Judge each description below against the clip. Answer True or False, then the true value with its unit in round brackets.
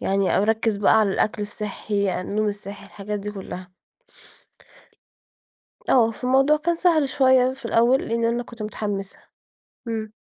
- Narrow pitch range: False (3.6 semitones)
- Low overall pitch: False (215 Hz)